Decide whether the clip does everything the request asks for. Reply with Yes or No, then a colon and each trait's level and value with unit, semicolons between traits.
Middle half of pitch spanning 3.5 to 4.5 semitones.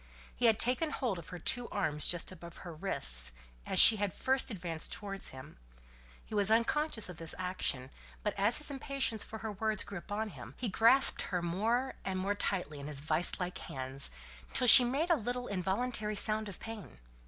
No: average, 5.3 semitones